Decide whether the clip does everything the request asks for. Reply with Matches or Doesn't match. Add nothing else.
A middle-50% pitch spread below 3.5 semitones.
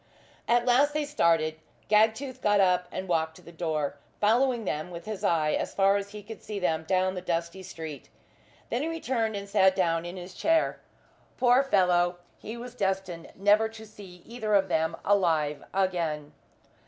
Doesn't match